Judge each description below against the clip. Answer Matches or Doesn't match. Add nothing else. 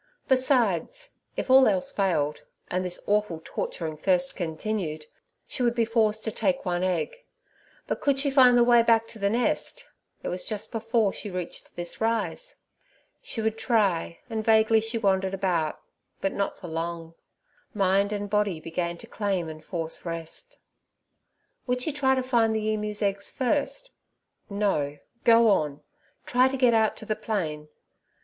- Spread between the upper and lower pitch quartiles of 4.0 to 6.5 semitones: Matches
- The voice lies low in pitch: Doesn't match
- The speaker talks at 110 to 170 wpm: Matches